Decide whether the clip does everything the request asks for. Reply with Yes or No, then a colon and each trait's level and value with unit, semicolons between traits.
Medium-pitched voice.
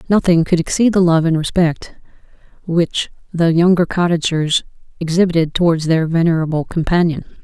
Yes: medium, 170 Hz